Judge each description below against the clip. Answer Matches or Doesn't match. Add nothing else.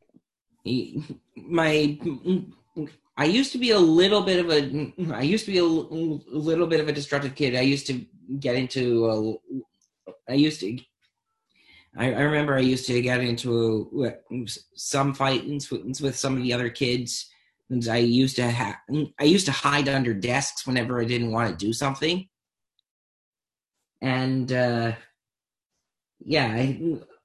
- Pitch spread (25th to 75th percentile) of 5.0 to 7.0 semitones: Doesn't match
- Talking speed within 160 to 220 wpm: Doesn't match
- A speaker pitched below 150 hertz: Matches